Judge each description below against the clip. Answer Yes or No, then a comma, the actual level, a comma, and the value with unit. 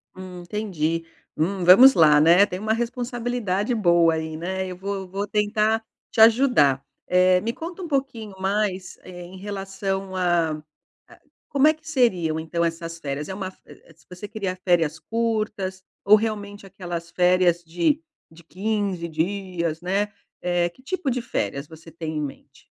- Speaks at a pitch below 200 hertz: Yes, medium, 185 Hz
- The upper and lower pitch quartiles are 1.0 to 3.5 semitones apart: No, average, 4.0 semitones